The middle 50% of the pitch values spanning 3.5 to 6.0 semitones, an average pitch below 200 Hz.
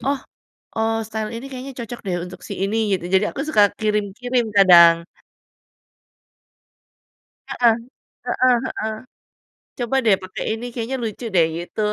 No: average, 3.8 semitones; high, 220 Hz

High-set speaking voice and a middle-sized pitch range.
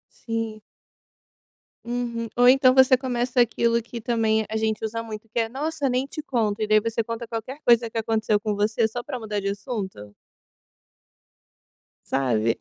No: high, 230 Hz; narrow, 2.2 semitones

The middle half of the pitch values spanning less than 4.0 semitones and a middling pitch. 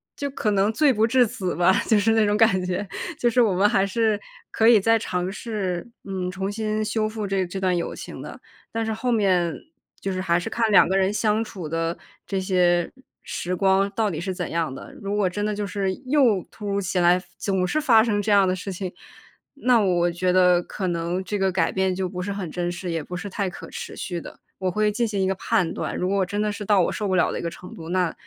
No: average, 2.8 semitones; high, 195 Hz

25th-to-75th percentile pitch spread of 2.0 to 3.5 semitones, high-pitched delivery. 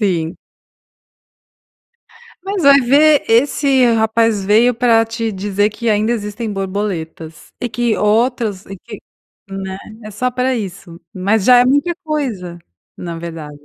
No: average, 4.3 semitones; high, 220 Hz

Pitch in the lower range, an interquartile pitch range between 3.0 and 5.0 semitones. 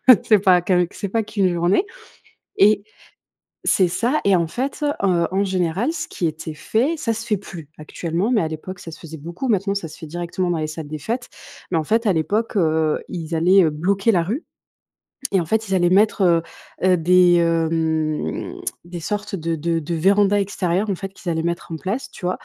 No: medium, 180 Hz; average, 3.6 semitones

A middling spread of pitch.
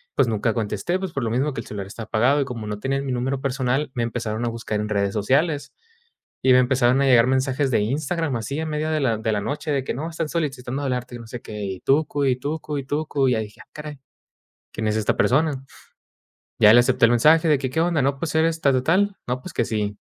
Yes: average, 4.2 semitones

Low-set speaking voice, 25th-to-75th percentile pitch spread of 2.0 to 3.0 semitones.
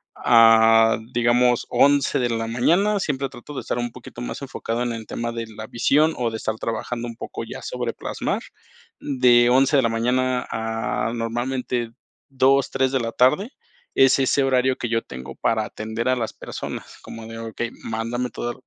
Yes: low, 120 Hz; narrow, 2.4 semitones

